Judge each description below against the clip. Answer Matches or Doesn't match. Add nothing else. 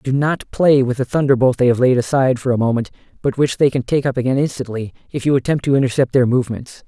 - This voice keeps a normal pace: Doesn't match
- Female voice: Doesn't match